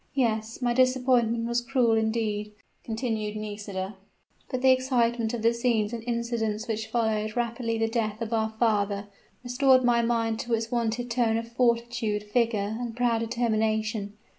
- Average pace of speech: Yes, average, 155 wpm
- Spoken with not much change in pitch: Yes, narrow, 1.7 semitones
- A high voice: Yes, high, 230 Hz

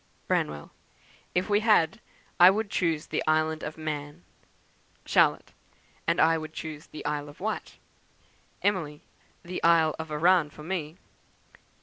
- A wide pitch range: No, average, 3.0 semitones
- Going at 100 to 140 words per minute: Yes, slow, 135 wpm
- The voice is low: No, medium, 160 Hz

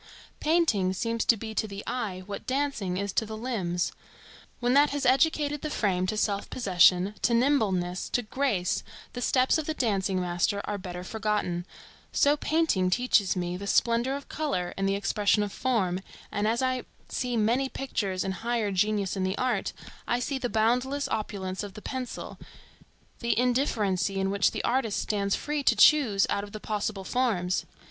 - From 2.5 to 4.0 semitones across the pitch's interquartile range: No, average, 4.8 semitones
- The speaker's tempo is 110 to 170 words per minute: No, average, 180 wpm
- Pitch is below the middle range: No, high, 215 Hz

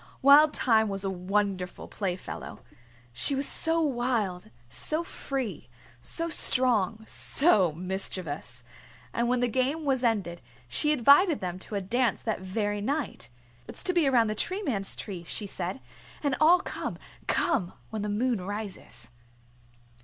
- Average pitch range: No, wide, 6.3 semitones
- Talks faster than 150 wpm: No, average, 145 wpm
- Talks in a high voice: Yes, high, 220 Hz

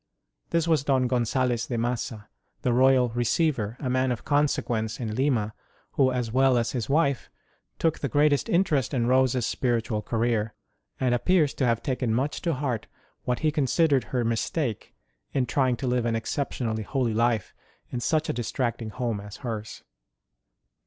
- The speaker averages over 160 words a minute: Yes, average, 175 wpm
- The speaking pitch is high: No, low, 125 Hz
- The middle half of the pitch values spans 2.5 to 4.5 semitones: Yes, average, 3.0 semitones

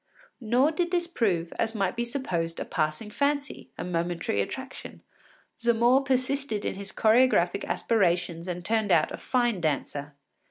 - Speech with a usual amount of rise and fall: No, wide, 6.9 semitones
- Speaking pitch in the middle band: No, high, 220 Hz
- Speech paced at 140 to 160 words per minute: Yes, average, 150 wpm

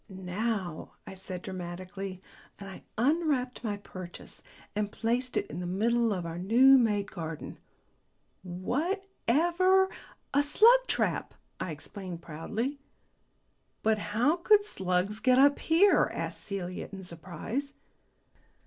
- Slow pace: Yes, slow, 125 wpm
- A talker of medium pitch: No, high, 210 Hz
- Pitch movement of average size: No, wide, 7.1 semitones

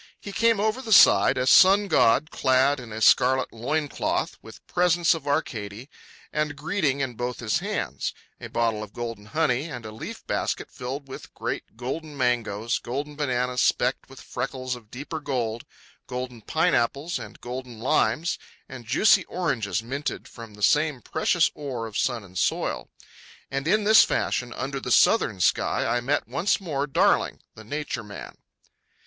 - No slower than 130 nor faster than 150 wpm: No, average, 165 wpm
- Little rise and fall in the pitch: No, average, 4.6 semitones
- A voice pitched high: No, low, 130 Hz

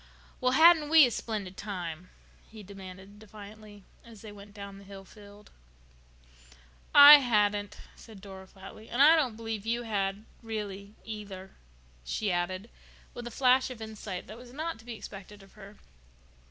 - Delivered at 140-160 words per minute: Yes, average, 155 wpm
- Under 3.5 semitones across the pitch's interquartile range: Yes, average, 2.8 semitones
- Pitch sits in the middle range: No, high, 210 Hz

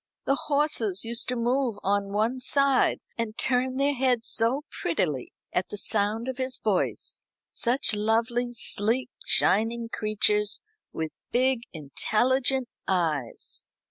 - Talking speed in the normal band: No, slow, 125 wpm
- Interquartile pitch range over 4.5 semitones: No, average, 3.8 semitones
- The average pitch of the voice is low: No, high, 230 Hz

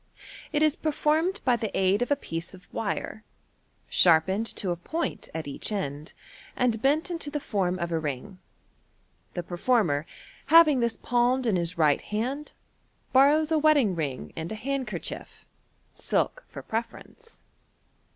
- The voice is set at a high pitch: Yes, high, 225 Hz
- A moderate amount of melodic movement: No, wide, 8.5 semitones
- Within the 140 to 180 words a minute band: Yes, average, 150 wpm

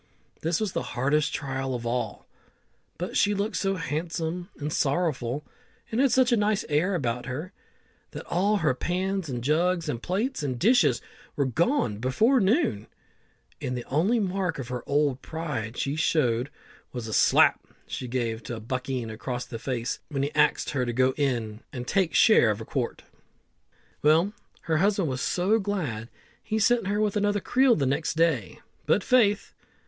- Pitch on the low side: No, medium, 150 Hz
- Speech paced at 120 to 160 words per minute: No, average, 175 wpm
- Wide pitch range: Yes, wide, 7.4 semitones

